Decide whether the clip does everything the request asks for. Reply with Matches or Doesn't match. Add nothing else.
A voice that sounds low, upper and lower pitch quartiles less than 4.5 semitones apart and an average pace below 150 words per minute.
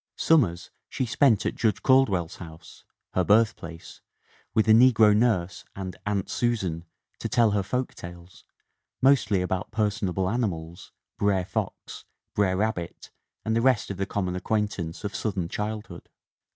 Matches